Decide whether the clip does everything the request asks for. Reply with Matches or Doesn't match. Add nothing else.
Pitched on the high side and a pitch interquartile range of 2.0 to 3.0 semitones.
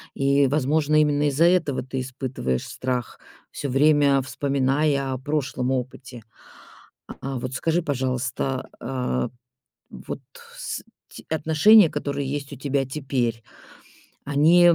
Doesn't match